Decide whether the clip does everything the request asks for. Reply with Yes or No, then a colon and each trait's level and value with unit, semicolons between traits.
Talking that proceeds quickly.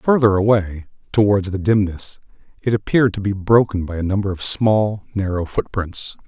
No: average, 165 wpm